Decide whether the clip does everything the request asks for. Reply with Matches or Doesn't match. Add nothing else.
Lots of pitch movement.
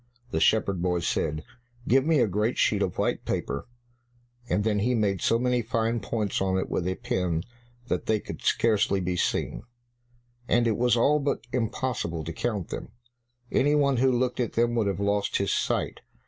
Doesn't match